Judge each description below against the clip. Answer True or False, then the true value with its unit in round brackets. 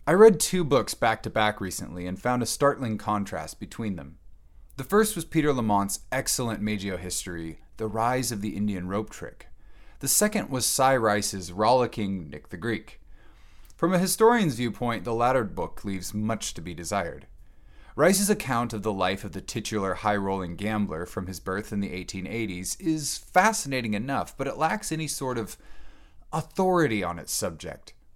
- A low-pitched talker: True (105 Hz)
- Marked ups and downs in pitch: True (5.8 semitones)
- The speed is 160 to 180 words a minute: True (175 wpm)